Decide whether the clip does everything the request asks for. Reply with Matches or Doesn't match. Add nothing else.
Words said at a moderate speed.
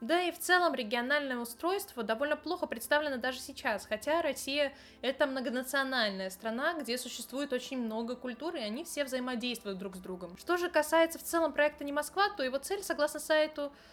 Doesn't match